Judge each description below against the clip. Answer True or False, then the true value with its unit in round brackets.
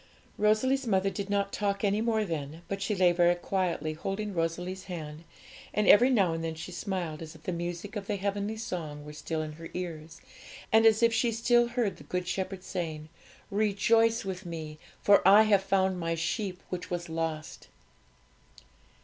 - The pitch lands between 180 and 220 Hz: True (190 Hz)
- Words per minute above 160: True (185 wpm)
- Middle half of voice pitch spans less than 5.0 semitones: True (3.9 semitones)